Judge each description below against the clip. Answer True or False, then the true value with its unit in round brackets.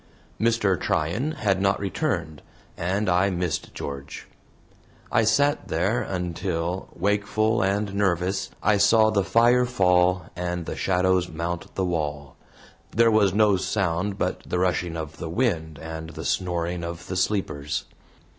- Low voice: True (95 Hz)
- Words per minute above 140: False (135 wpm)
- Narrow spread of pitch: False (3.6 semitones)